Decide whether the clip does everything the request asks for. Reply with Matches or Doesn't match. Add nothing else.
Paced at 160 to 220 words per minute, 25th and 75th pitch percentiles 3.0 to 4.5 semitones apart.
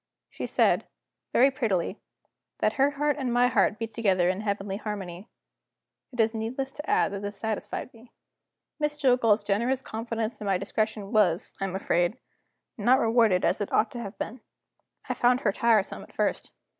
Matches